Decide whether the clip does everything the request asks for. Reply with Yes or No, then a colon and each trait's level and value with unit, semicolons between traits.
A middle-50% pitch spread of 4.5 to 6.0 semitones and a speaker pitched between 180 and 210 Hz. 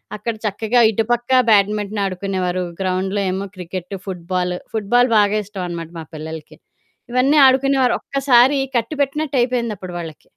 Yes: average, 4.9 semitones; high, 205 Hz